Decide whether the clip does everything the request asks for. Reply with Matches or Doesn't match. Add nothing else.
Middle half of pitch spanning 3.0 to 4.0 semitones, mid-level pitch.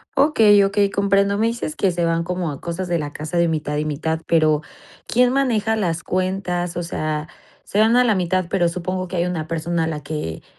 Matches